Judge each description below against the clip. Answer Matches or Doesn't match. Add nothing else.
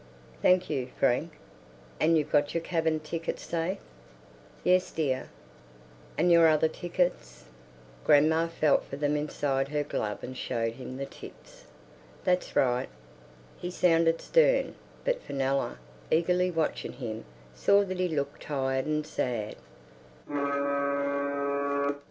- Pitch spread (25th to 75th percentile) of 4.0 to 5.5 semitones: Matches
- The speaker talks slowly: Matches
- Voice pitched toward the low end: Doesn't match